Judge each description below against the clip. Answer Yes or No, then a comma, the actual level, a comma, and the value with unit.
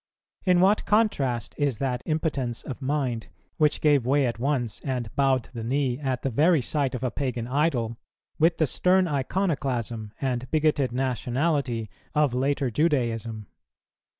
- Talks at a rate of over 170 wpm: No, average, 150 wpm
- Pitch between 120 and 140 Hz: Yes, low, 135 Hz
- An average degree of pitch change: Yes, average, 3.8 semitones